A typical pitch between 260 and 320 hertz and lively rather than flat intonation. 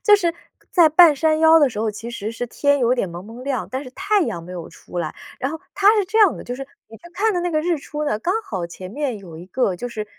Yes: very high, 265 Hz; wide, 7.8 semitones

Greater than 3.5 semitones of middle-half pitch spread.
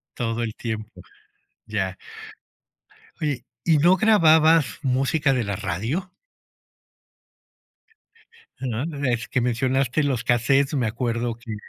Yes: average, 4.0 semitones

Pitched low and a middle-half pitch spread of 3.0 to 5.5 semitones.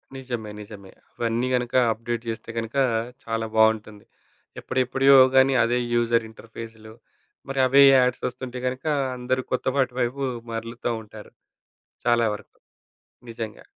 No: low, 120 Hz; narrow, 2.4 semitones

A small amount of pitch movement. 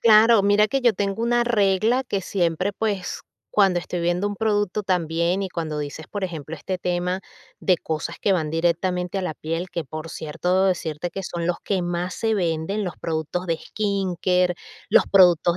No: average, 3.0 semitones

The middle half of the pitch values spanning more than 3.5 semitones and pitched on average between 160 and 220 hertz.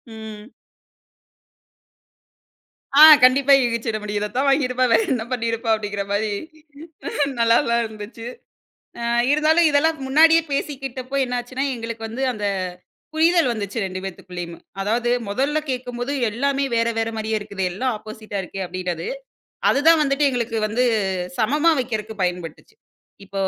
No: average, 4.3 semitones; high, 235 Hz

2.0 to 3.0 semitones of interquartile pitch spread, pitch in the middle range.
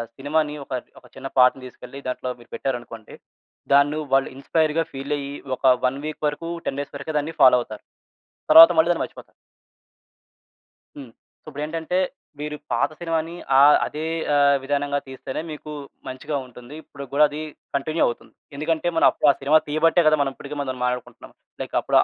Yes: narrow, 2.6 semitones; medium, 145 Hz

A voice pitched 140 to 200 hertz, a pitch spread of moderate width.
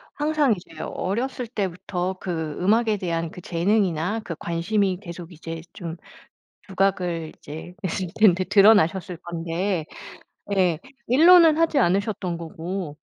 Yes: medium, 185 Hz; average, 3.9 semitones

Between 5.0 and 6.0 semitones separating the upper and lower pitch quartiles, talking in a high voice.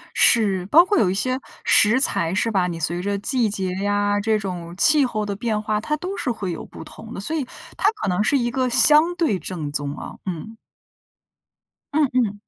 Yes: average, 5.3 semitones; high, 210 Hz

